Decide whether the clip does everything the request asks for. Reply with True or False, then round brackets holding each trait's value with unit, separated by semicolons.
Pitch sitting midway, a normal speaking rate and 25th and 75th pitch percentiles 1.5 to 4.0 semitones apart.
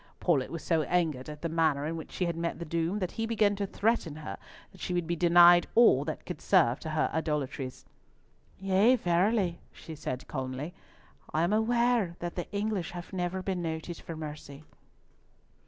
True (170 Hz; 190 wpm; 3.4 semitones)